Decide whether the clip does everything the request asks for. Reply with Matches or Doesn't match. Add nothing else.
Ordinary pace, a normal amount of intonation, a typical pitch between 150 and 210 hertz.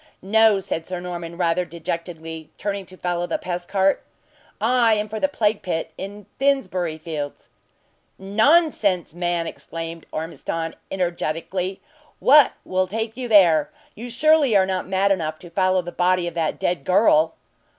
Matches